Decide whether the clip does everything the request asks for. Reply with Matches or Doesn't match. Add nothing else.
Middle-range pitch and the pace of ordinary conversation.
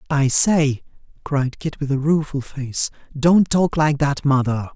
Matches